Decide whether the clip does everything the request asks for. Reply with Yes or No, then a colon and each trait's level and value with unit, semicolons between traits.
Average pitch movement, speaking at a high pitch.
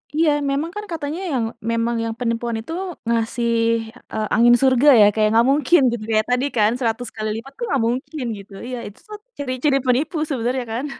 Yes: average, 3.7 semitones; high, 245 Hz